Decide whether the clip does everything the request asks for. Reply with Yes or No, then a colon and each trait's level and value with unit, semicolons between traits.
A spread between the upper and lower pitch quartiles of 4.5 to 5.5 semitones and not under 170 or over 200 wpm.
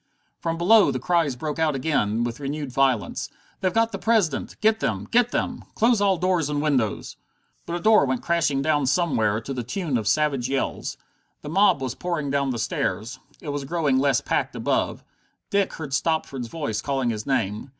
Yes: average, 4.8 semitones; average, 190 wpm